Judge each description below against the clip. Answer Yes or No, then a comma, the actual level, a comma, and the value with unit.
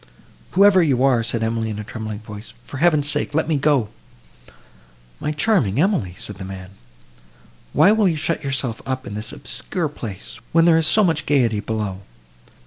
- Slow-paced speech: No, average, 180 wpm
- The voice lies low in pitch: Yes, low, 130 Hz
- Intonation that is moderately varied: No, wide, 6.9 semitones